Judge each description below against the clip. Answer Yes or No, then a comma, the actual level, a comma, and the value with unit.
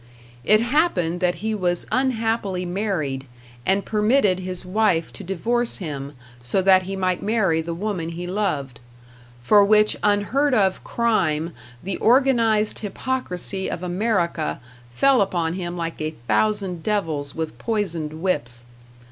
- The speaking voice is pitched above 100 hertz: Yes, high, 190 Hz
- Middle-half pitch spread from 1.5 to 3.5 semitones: No, average, 4.2 semitones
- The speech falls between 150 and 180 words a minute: No, slow, 135 wpm